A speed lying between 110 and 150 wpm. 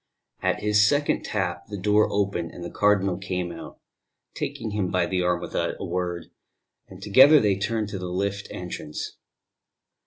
No: average, 165 wpm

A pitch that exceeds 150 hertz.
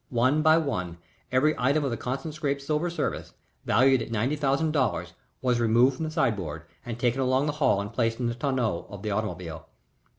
No: low, 130 Hz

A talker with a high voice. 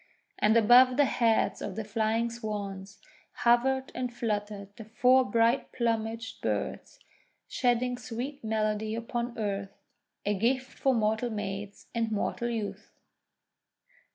Yes: high, 230 Hz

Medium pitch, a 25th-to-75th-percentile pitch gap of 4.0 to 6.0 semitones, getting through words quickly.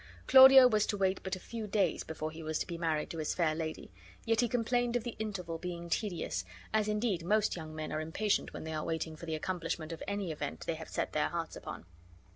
Yes: medium, 175 Hz; average, 5.1 semitones; fast, 240 wpm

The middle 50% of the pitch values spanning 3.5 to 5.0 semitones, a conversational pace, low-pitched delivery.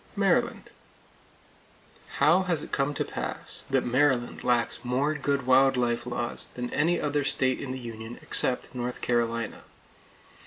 No: average, 2.8 semitones; average, 145 wpm; low, 130 Hz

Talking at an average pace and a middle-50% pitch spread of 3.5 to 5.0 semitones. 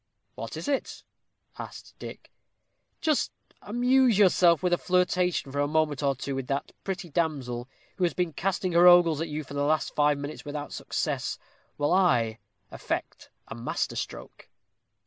Yes: average, 165 wpm; average, 4.1 semitones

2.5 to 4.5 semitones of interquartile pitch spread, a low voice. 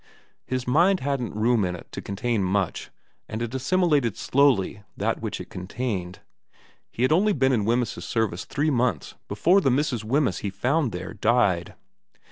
No: wide, 5.4 semitones; low, 120 Hz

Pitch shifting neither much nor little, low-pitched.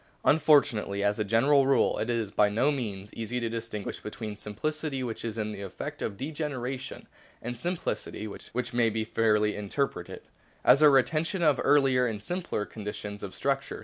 Yes: average, 4.6 semitones; low, 115 Hz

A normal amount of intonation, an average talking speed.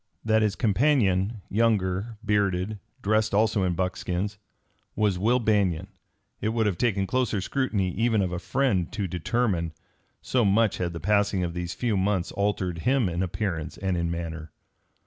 Yes: average, 3.5 semitones; average, 160 wpm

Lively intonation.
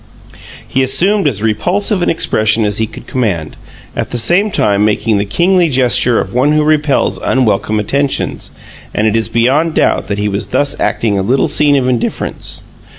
Yes: wide, 5.8 semitones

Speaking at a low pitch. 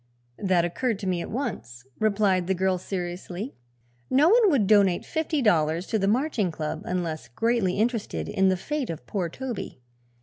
No: high, 190 Hz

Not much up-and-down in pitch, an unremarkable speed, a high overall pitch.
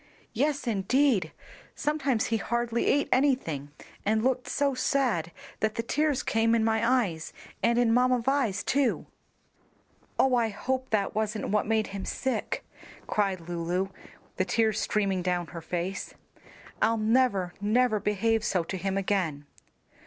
No: average, 4.6 semitones; average, 145 wpm; high, 220 Hz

